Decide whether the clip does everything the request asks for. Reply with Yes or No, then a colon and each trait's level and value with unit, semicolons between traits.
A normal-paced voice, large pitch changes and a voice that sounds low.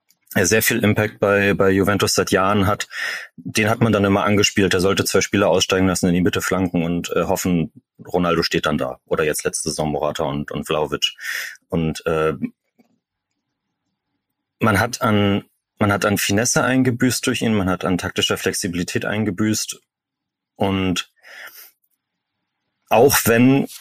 No: average, 155 wpm; average, 2.8 semitones; low, 100 Hz